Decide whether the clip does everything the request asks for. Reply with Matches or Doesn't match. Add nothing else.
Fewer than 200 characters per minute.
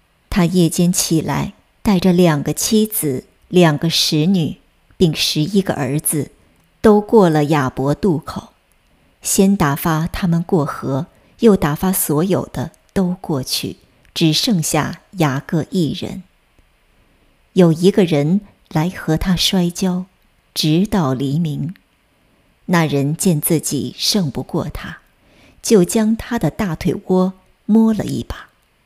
Matches